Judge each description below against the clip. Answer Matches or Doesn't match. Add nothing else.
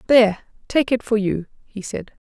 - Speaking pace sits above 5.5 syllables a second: Doesn't match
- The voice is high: Matches